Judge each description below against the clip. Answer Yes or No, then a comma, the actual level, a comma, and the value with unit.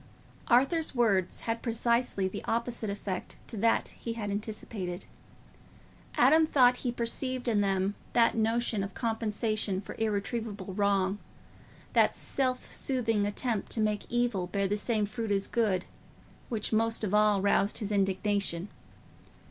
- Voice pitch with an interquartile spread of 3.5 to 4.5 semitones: No, average, 2.8 semitones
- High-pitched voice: Yes, high, 215 Hz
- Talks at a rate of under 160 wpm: Yes, average, 140 wpm